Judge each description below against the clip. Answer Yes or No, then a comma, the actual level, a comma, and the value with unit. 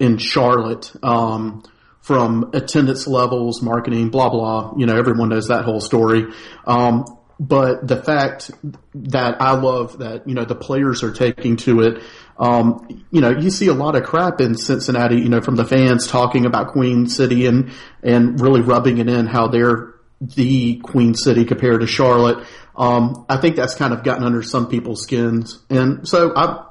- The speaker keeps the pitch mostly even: Yes, narrow, 2.1 semitones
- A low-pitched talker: Yes, low, 120 Hz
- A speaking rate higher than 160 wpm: Yes, average, 180 wpm